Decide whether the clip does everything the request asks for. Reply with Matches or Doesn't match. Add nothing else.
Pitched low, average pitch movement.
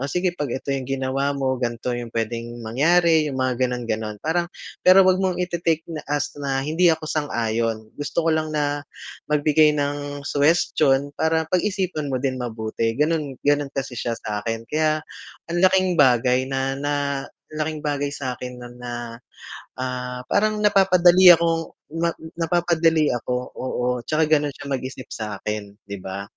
Doesn't match